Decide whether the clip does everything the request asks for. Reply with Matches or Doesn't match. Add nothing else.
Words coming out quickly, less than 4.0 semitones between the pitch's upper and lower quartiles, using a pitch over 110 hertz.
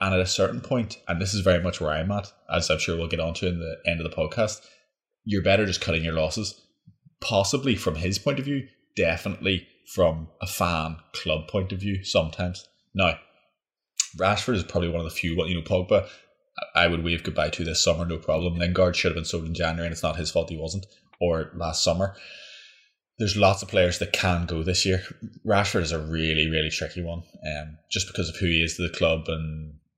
Doesn't match